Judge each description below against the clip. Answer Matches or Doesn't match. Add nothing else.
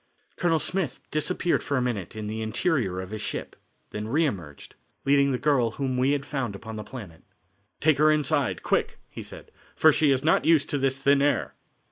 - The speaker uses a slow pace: Doesn't match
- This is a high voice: Doesn't match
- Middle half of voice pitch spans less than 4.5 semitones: Doesn't match